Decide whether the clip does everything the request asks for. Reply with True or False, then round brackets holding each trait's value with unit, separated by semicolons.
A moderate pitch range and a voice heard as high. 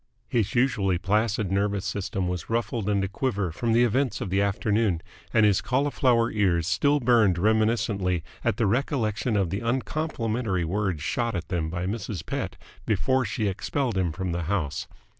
False (3.9 semitones; 105 Hz)